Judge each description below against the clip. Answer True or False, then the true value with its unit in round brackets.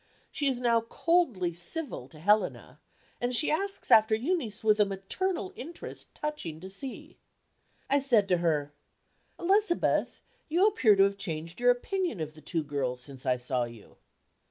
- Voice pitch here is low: False (215 Hz)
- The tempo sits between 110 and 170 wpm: True (160 wpm)